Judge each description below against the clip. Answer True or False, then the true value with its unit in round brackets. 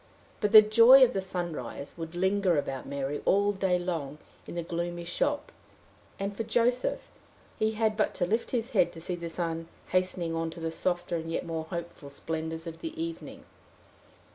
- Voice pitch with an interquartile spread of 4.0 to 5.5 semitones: True (4.4 semitones)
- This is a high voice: False (175 Hz)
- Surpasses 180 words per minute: True (190 wpm)